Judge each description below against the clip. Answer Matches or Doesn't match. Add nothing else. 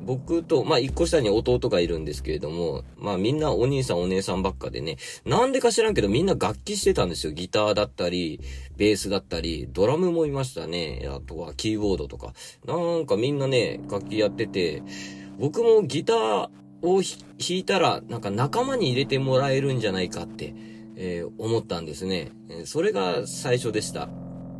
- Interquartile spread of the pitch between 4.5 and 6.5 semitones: Doesn't match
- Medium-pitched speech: Doesn't match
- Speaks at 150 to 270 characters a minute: Doesn't match